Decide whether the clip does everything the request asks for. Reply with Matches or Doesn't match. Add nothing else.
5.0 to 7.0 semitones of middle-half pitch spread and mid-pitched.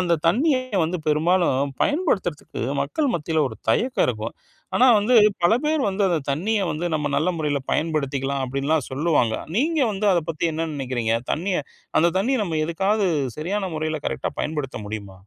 Matches